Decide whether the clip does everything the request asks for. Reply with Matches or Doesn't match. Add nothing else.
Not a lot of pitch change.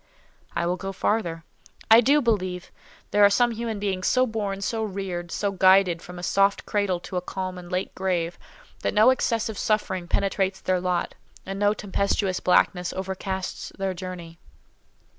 Matches